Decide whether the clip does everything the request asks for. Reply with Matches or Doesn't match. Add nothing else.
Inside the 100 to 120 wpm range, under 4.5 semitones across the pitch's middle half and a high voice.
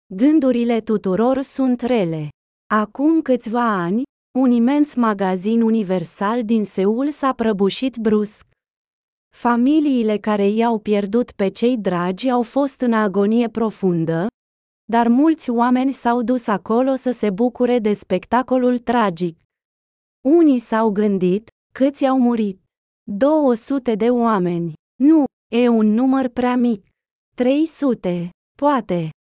Matches